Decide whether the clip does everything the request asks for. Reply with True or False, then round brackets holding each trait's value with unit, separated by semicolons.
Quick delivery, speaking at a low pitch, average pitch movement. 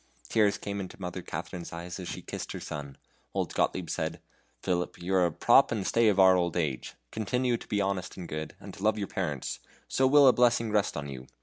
True (225 wpm; 95 Hz; 3.9 semitones)